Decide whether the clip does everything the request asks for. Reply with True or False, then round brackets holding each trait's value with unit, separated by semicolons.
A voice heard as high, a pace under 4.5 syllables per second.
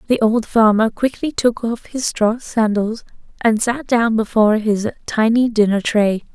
True (225 Hz; 4.3 syllables/s)